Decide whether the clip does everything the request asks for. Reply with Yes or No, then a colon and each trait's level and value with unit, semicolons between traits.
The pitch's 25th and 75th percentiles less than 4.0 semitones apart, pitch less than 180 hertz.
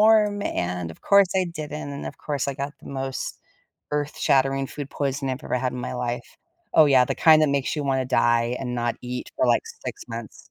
Yes: average, 3.3 semitones; low, 135 Hz